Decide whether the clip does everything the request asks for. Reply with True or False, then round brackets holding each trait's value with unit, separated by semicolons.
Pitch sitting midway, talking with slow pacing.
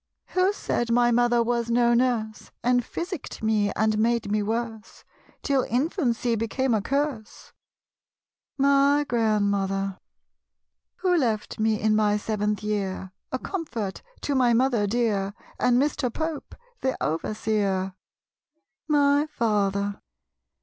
False (230 Hz; 120 wpm)